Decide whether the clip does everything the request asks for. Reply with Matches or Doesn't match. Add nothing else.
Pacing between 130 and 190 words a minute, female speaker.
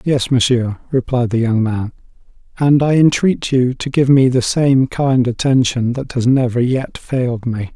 Doesn't match